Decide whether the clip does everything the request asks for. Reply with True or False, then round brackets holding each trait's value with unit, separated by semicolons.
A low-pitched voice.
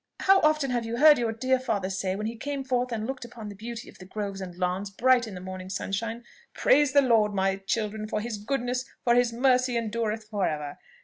False (225 Hz)